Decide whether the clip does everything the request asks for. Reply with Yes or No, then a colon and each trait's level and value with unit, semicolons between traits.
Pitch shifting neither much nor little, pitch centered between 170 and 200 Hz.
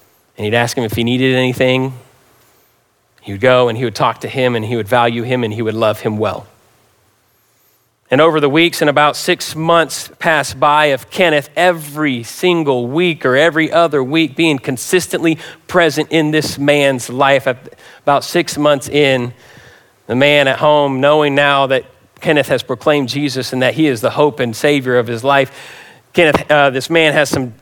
No: average, 3.4 semitones; medium, 140 Hz